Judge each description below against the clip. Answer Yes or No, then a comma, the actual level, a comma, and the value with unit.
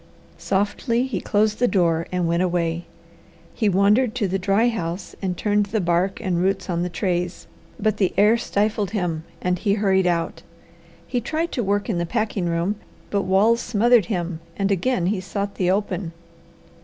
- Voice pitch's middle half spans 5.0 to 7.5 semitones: No, average, 3.2 semitones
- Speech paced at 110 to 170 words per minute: No, average, 180 wpm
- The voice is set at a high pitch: Yes, high, 195 Hz